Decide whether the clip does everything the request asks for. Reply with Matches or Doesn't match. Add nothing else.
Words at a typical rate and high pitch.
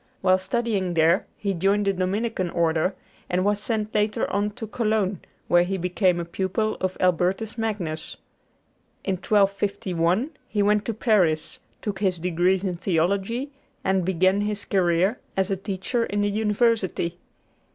Matches